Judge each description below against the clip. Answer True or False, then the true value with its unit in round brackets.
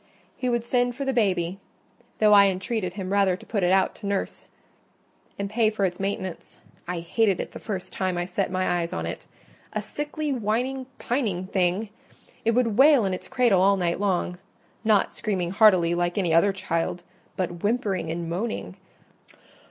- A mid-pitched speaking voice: False (195 Hz)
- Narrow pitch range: False (3.9 semitones)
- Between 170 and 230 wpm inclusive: True (175 wpm)